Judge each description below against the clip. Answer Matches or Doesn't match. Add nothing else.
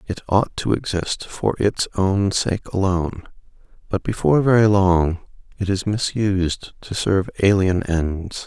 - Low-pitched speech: Matches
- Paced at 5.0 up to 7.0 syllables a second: Doesn't match